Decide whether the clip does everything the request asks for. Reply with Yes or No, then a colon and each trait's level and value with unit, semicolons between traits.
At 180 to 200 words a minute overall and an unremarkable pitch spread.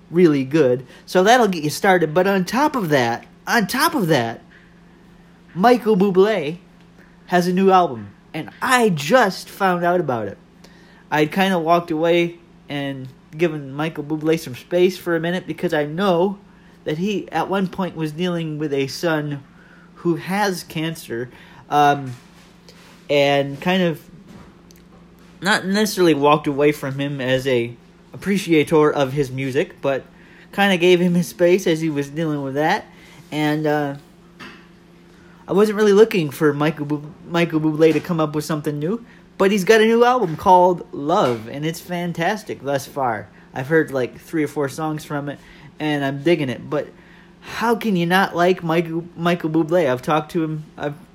No: average, 170 wpm; average, 3.4 semitones